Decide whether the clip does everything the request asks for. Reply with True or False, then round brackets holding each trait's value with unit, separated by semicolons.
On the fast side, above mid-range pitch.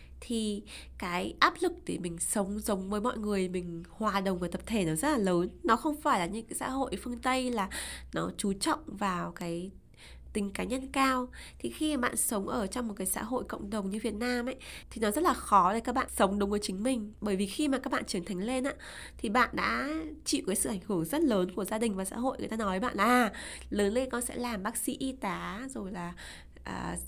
True (255 wpm; 215 Hz)